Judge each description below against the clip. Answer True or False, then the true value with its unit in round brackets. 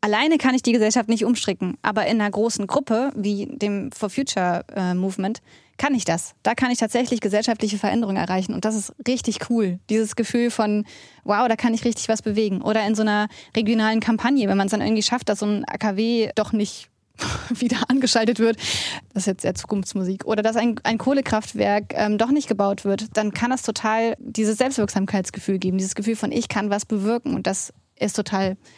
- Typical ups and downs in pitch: False (2.3 semitones)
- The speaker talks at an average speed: False (200 wpm)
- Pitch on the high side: True (215 Hz)